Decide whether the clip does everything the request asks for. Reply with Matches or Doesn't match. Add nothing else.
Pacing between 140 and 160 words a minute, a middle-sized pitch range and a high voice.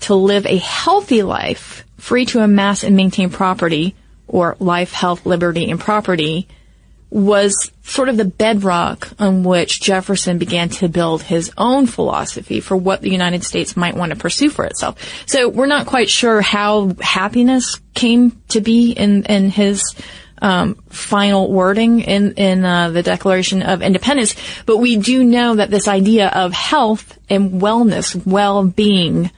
Matches